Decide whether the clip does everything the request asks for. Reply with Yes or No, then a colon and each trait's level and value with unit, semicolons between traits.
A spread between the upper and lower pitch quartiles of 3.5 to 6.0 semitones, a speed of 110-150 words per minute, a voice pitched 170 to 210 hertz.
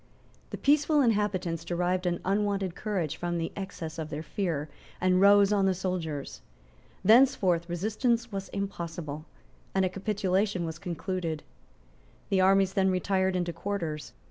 No: average, 2.9 semitones; average, 140 wpm; medium, 185 Hz